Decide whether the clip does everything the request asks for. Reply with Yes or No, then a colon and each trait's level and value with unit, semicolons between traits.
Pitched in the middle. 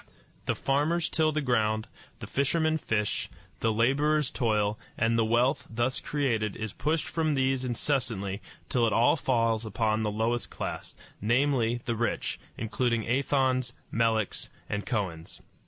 No: low, 120 Hz